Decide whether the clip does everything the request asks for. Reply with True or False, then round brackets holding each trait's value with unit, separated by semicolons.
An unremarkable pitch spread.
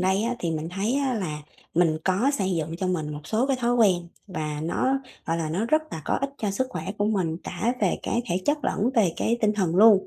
False (5.8 semitones)